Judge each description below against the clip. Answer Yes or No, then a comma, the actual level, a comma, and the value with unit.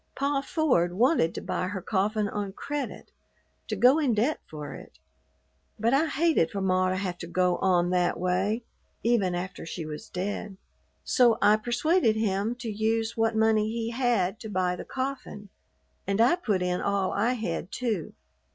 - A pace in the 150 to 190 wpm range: Yes, average, 175 wpm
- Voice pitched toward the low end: No, high, 210 Hz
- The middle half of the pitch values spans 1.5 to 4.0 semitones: No, average, 4.5 semitones